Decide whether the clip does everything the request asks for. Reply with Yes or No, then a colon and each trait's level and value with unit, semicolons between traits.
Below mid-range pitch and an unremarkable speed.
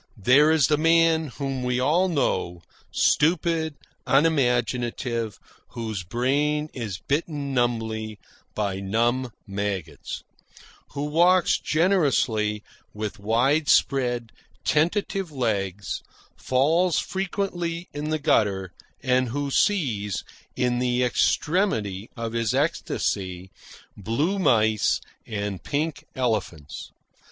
No: low, 125 Hz; slow, 100 wpm